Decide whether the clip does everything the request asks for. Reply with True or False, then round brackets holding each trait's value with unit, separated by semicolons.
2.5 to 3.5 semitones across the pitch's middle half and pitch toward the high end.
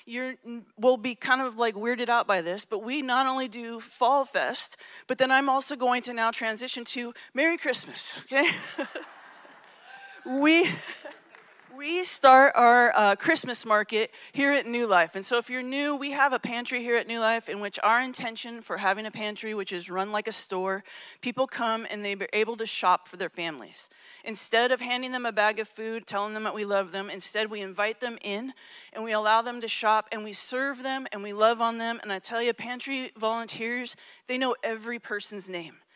True (3.1 semitones; 230 Hz)